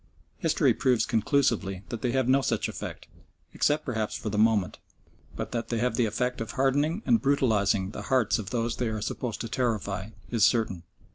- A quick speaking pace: No, average, 190 wpm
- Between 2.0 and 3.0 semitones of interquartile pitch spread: No, average, 3.4 semitones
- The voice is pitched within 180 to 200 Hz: No, low, 115 Hz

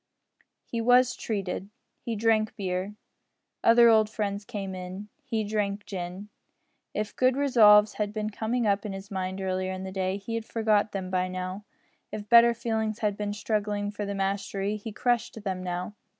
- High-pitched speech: Yes, high, 205 Hz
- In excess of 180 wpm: No, average, 165 wpm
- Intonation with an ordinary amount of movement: No, narrow, 2.3 semitones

